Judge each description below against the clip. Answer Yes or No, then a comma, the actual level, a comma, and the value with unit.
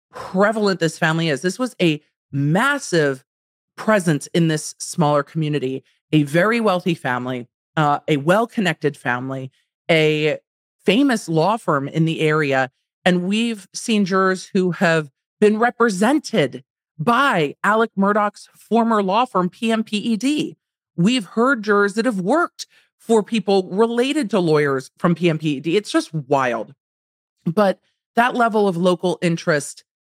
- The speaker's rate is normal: No, slow, 130 wpm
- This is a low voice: No, medium, 180 Hz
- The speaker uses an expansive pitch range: Yes, wide, 6.1 semitones